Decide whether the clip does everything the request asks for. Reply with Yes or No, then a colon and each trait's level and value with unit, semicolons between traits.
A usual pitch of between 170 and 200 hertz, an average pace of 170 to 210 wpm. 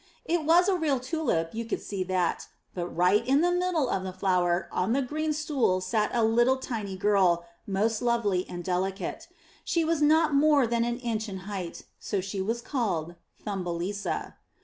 No: high, 220 Hz; average, 185 wpm